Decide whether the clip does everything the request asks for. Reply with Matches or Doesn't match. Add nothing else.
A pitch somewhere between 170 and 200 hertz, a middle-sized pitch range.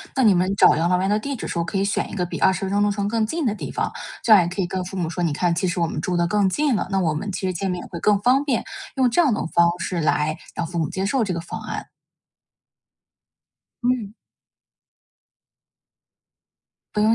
Matches